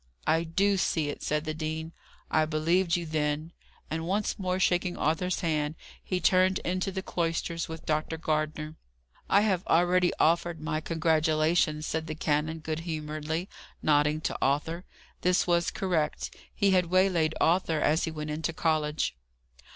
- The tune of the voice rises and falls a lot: No, narrow, 2.4 semitones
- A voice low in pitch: No, medium, 160 Hz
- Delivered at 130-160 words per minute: Yes, average, 155 wpm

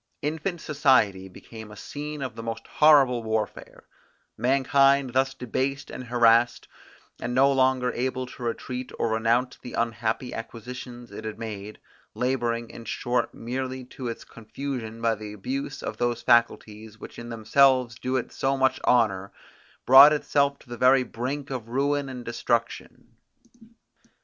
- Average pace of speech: Yes, average, 150 wpm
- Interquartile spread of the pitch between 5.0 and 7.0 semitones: No, average, 2.7 semitones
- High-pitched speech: No, low, 125 Hz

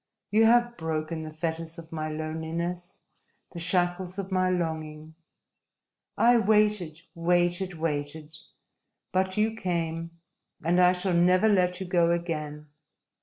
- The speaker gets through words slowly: Yes, slow, 125 wpm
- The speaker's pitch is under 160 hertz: No, medium, 175 Hz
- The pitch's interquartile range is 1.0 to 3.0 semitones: Yes, narrow, 2.5 semitones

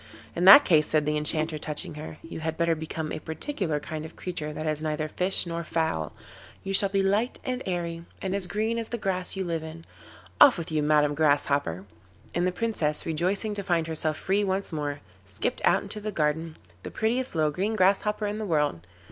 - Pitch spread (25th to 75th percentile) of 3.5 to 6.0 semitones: Yes, average, 4.2 semitones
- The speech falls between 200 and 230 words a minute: Yes, fast, 205 wpm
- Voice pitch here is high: No, medium, 165 Hz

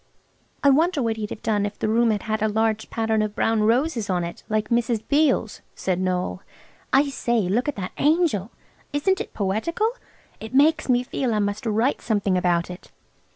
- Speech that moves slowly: No, average, 195 wpm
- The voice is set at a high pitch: Yes, high, 220 Hz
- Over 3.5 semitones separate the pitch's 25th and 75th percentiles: Yes, average, 4.5 semitones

